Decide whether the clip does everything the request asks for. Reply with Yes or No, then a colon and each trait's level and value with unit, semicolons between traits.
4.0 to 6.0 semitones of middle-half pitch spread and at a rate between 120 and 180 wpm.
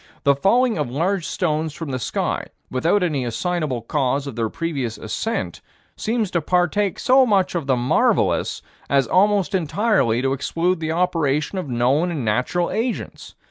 Yes: wide, 5.5 semitones; average, 160 wpm